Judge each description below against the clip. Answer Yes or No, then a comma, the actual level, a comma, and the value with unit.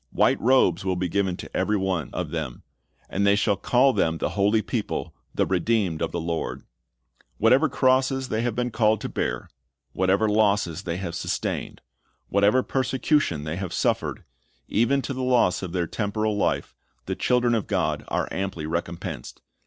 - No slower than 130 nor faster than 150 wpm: No, average, 170 wpm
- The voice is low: Yes, low, 100 Hz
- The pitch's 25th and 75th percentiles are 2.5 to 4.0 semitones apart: No, wide, 5.4 semitones